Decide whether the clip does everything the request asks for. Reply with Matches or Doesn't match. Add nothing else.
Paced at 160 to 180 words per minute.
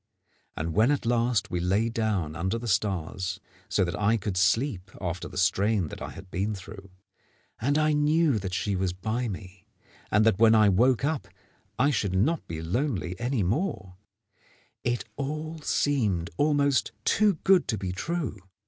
Matches